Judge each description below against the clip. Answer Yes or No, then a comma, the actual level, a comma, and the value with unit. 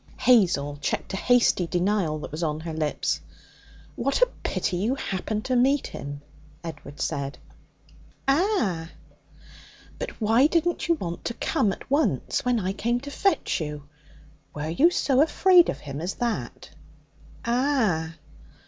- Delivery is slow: No, average, 145 wpm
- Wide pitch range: Yes, wide, 9.0 semitones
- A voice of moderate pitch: No, high, 210 Hz